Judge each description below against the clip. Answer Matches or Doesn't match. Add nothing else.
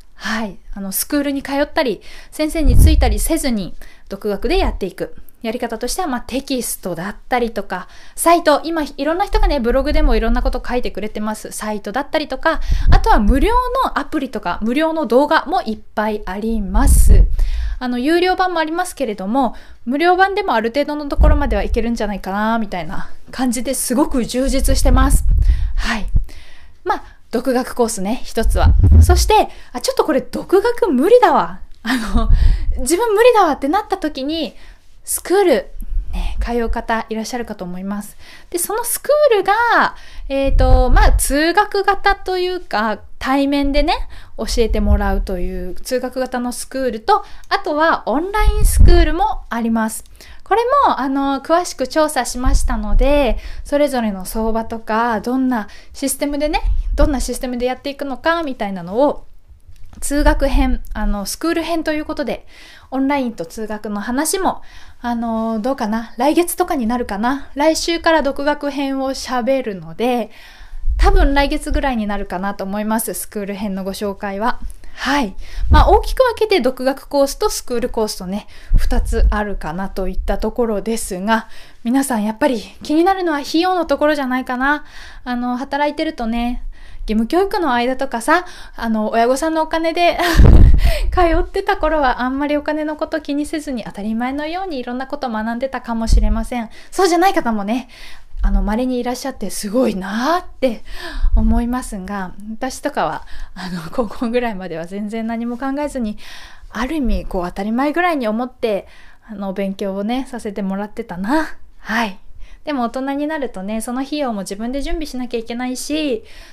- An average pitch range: Doesn't match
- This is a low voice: Doesn't match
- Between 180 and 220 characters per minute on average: Doesn't match